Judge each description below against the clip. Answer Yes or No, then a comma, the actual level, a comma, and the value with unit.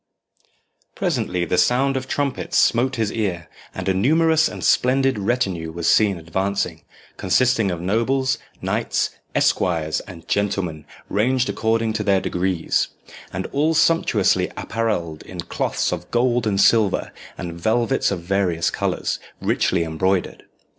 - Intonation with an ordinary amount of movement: No, wide, 5.9 semitones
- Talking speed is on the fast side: No, slow, 135 wpm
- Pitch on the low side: Yes, low, 100 Hz